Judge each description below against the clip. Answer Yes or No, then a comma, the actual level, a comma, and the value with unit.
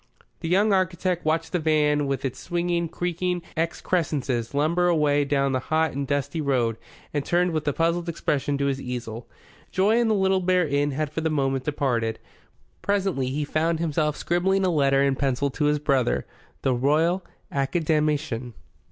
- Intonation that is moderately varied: Yes, average, 3.9 semitones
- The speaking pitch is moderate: Yes, medium, 150 Hz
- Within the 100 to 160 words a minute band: No, average, 170 wpm